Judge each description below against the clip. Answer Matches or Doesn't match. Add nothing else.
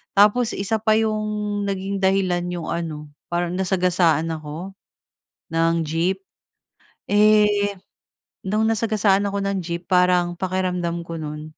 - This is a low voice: Doesn't match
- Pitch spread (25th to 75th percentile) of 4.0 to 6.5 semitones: Doesn't match